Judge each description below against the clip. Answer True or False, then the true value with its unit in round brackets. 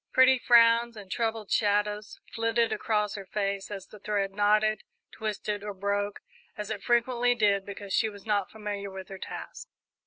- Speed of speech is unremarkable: True (165 wpm)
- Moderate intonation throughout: False (2.0 semitones)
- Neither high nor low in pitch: False (210 Hz)